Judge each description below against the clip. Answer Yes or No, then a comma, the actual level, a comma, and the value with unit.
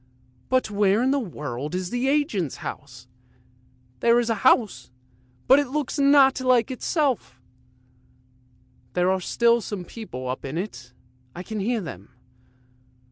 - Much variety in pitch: Yes, wide, 7.2 semitones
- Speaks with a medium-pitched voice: No, high, 215 Hz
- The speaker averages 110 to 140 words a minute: Yes, slow, 135 wpm